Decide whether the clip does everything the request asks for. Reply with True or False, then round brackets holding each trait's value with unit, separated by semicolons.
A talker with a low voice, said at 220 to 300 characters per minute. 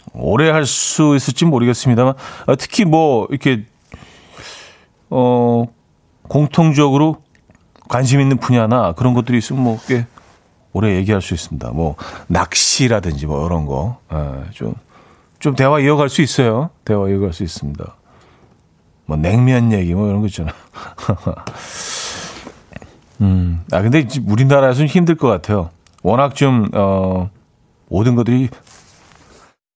True (120 Hz; 250 characters per minute)